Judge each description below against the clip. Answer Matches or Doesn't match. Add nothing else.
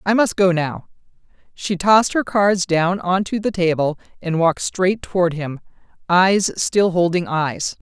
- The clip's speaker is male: Doesn't match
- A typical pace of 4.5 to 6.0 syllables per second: Doesn't match